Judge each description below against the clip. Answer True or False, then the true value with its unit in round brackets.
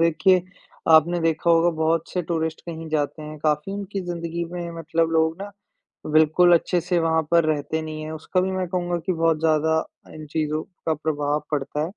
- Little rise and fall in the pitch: True (1.7 semitones)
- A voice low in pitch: False (160 Hz)